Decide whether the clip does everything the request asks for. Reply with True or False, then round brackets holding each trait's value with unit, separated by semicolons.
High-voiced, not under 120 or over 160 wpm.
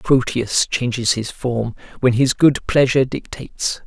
False (125 Hz; 140 wpm)